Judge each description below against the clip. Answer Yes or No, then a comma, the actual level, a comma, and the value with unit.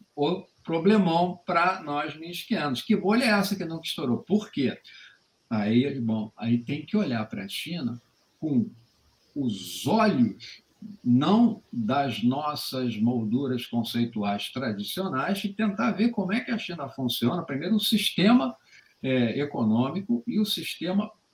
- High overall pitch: No, medium, 170 Hz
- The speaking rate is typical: Yes, average, 140 wpm